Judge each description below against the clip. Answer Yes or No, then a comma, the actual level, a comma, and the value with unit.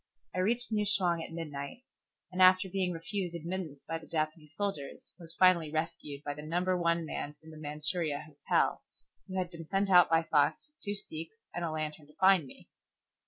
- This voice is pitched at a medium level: Yes, medium, 165 Hz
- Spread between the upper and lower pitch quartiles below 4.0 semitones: Yes, average, 3.2 semitones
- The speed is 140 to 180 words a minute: No, average, 195 wpm